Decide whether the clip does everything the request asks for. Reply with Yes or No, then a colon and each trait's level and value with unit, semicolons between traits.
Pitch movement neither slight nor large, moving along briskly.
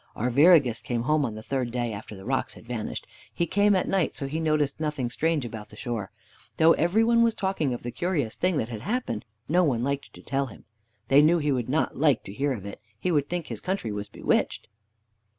No: wide, 5.8 semitones; fast, 230 wpm